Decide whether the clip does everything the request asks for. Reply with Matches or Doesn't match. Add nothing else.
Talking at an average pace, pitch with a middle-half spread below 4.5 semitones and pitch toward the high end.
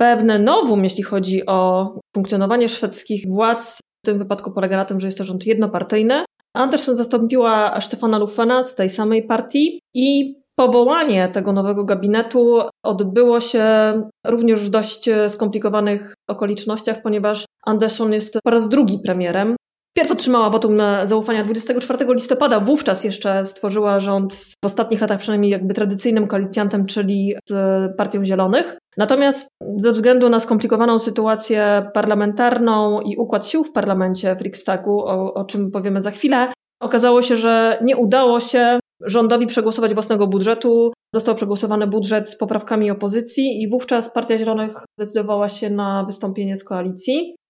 Matches